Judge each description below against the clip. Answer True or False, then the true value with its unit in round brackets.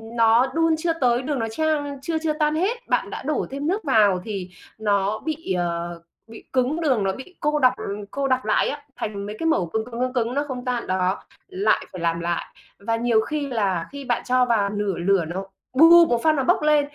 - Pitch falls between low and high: False (250 Hz)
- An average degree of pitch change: False (6.7 semitones)